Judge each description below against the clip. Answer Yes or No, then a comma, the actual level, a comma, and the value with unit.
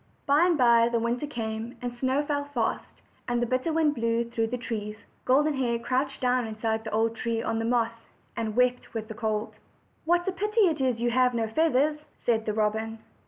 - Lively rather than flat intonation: No, average, 3.3 semitones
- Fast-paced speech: Yes, fast, 210 wpm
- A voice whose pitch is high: Yes, high, 240 Hz